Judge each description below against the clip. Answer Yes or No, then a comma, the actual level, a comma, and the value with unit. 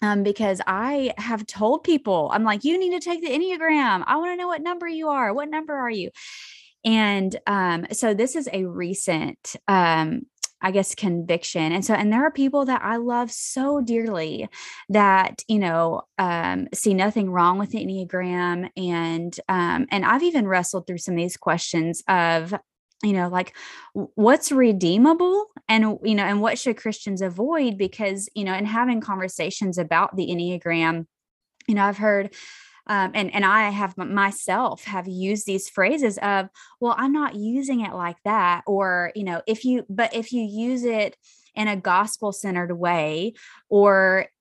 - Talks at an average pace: Yes, average, 175 wpm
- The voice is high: Yes, high, 205 Hz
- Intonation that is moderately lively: Yes, average, 4.6 semitones